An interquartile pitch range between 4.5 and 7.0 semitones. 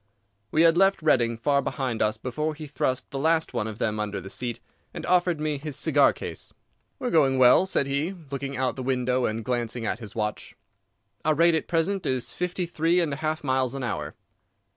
Yes: average, 4.9 semitones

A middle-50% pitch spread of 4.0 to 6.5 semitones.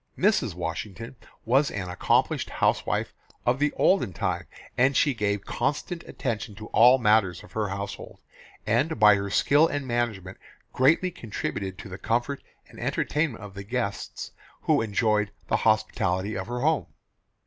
Yes: average, 5.1 semitones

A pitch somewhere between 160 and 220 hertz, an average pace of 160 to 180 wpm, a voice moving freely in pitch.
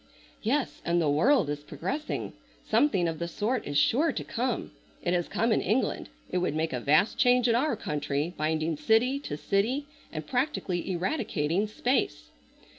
Yes: high, 190 Hz; average, 170 wpm; wide, 8.1 semitones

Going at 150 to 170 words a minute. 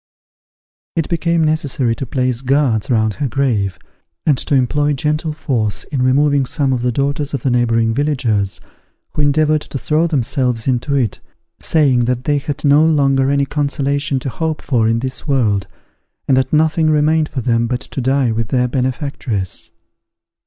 Yes: average, 165 wpm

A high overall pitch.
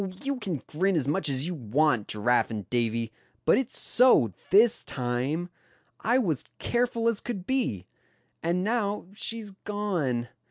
No: medium, 175 Hz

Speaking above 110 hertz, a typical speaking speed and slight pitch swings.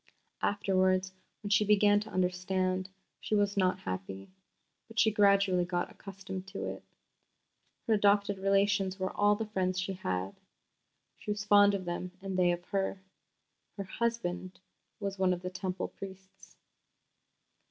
Yes: high, 190 Hz; average, 145 wpm; narrow, 1.7 semitones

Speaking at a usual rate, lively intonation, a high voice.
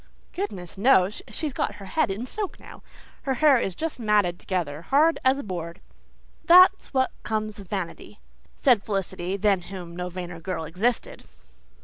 Yes: average, 160 wpm; wide, 6.5 semitones; high, 200 Hz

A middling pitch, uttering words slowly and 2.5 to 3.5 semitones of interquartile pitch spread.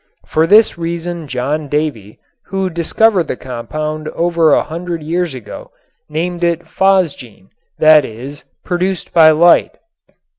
Yes: medium, 160 Hz; slow, 125 wpm; average, 2.9 semitones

